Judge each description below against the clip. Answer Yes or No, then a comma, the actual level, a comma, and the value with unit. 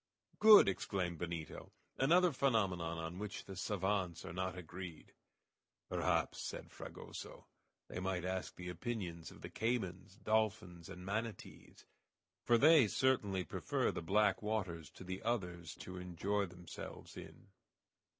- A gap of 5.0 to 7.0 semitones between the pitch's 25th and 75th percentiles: No, average, 3.6 semitones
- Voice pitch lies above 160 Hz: No, very low, 95 Hz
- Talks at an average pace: No, slow, 130 wpm